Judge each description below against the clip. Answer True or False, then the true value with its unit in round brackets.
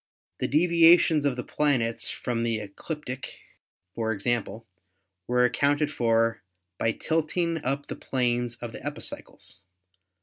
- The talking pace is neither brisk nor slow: False (125 wpm)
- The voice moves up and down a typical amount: True (4.6 semitones)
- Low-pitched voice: True (125 Hz)